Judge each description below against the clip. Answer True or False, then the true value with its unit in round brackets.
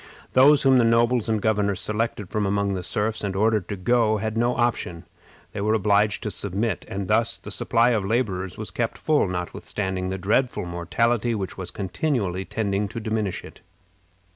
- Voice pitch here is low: True (105 Hz)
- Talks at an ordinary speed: True (180 wpm)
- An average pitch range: True (3.2 semitones)